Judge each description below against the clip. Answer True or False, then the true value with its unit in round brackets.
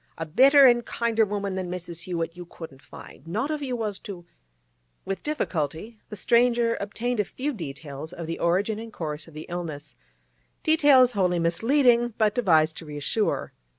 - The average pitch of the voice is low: False (190 Hz)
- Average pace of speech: True (165 wpm)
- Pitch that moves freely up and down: True (6.3 semitones)